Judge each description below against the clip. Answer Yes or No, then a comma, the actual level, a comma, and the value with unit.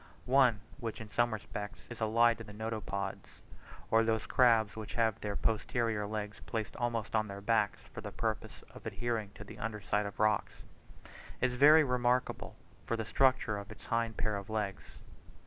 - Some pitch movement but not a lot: No, narrow, 2.1 semitones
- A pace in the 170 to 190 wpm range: Yes, average, 180 wpm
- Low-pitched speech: Yes, low, 110 Hz